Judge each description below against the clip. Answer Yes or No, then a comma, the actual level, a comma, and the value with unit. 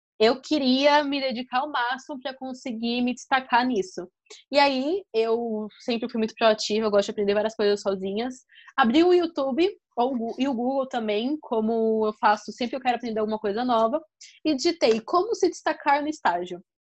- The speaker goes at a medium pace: Yes, average, 175 wpm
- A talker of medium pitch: No, high, 245 Hz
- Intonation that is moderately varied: Yes, average, 4.5 semitones